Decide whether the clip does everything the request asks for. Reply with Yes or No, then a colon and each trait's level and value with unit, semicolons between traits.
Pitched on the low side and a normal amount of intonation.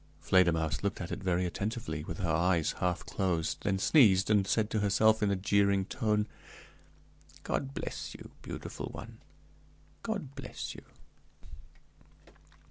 Yes: low, 100 Hz; average, 3.3 semitones